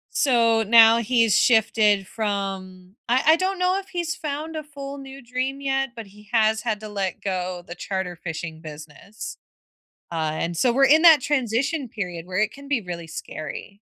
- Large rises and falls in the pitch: Yes, wide, 6.6 semitones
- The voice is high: Yes, high, 225 Hz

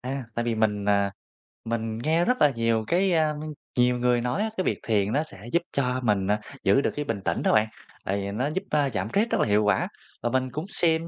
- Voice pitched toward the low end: Yes, low, 125 Hz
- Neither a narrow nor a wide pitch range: No, wide, 6.0 semitones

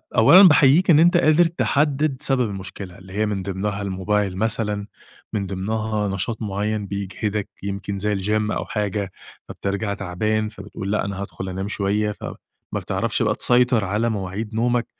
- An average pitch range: No, narrow, 2.3 semitones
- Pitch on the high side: No, low, 105 Hz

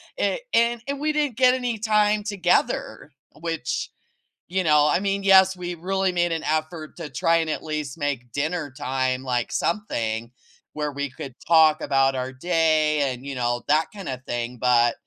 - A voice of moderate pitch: Yes, medium, 155 Hz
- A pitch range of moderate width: No, wide, 6.2 semitones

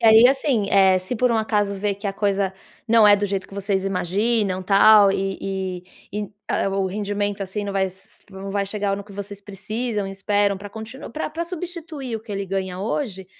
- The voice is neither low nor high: No, high, 200 Hz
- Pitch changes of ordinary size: No, narrow, 2.1 semitones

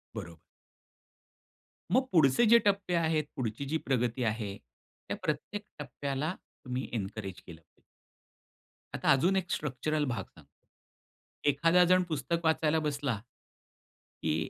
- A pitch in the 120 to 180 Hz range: Yes, medium, 140 Hz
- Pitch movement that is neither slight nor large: No, wide, 6.5 semitones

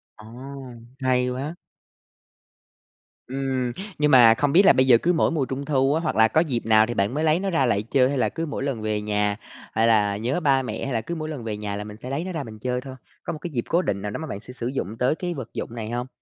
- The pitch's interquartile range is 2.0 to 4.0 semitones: No, average, 4.6 semitones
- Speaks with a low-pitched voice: Yes, low, 125 Hz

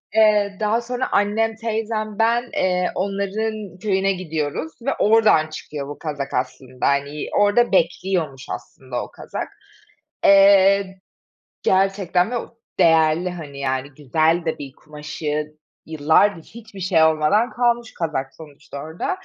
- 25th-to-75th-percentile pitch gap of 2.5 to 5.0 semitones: No, wide, 5.6 semitones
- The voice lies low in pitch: No, medium, 185 Hz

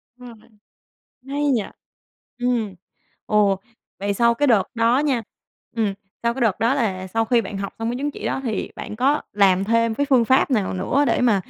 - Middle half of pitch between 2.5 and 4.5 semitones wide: Yes, average, 3.6 semitones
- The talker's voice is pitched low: No, high, 230 Hz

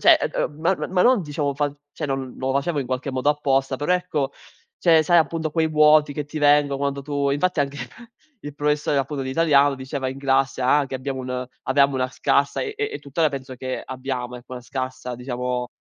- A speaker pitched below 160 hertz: Yes, medium, 140 Hz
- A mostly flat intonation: Yes, narrow, 2.2 semitones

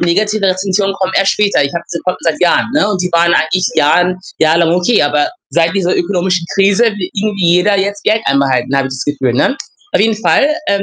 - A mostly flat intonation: No, average, 3.4 semitones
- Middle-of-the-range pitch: Yes, medium, 180 Hz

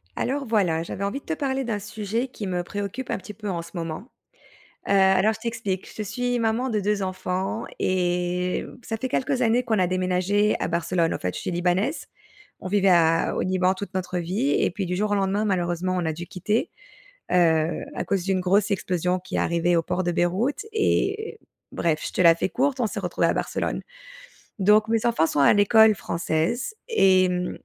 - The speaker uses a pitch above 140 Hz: Yes, high, 190 Hz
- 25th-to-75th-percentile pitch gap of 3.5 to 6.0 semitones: Yes, average, 3.8 semitones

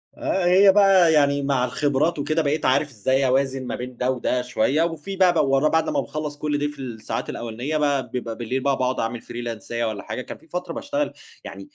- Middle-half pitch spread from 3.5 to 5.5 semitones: Yes, average, 3.8 semitones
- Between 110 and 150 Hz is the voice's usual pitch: Yes, medium, 140 Hz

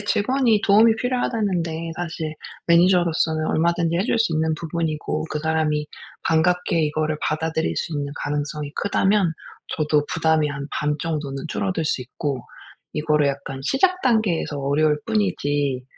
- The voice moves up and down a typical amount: Yes, average, 3.2 semitones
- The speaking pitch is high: No, medium, 160 Hz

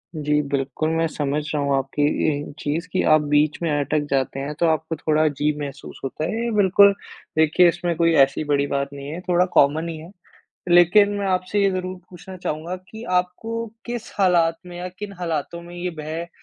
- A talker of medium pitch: Yes, medium, 165 Hz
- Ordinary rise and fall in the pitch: Yes, average, 3.5 semitones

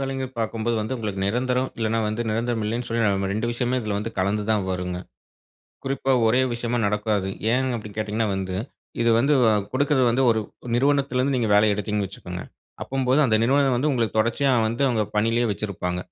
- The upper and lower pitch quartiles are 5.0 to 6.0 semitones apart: No, average, 3.4 semitones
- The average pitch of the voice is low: Yes, low, 115 Hz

